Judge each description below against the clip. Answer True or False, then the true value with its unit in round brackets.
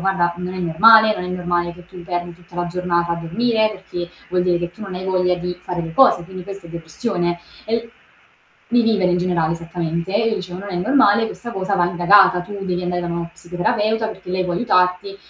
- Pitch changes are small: True (2.3 semitones)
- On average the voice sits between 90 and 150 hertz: False (180 Hz)